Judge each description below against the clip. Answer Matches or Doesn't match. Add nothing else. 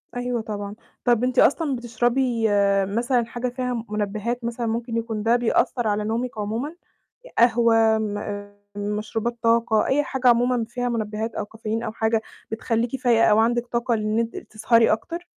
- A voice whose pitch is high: Matches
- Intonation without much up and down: Matches